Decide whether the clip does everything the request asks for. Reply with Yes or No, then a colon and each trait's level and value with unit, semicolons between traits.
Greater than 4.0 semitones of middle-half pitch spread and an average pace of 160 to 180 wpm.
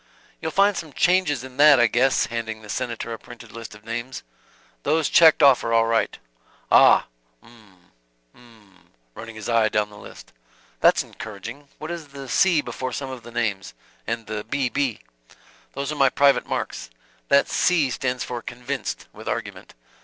No: average, 3.7 semitones; average, 175 wpm